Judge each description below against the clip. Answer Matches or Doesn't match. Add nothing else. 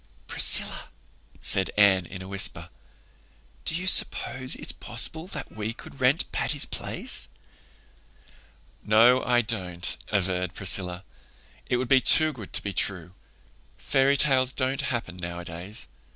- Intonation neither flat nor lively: Doesn't match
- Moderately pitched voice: Doesn't match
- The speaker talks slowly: Matches